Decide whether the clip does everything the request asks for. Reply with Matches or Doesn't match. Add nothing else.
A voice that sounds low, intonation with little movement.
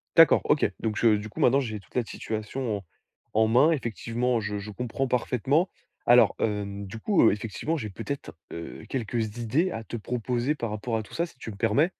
Doesn't match